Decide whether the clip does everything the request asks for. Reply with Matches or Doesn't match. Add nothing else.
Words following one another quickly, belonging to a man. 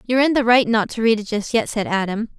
Doesn't match